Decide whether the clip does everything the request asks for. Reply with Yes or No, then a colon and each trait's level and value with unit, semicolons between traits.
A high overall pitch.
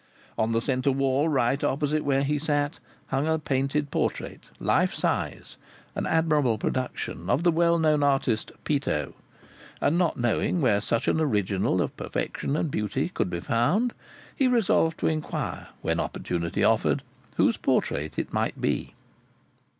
No: medium, 140 Hz